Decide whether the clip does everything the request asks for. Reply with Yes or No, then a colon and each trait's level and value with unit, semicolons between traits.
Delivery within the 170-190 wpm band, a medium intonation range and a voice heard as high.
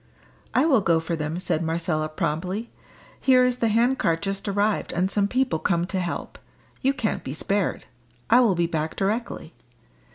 No: average, 175 wpm; wide, 5.7 semitones; high, 195 Hz